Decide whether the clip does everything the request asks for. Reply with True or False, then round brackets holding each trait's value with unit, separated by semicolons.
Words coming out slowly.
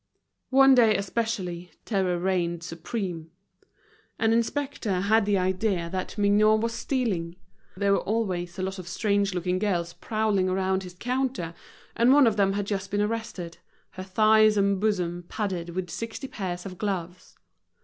False (155 wpm)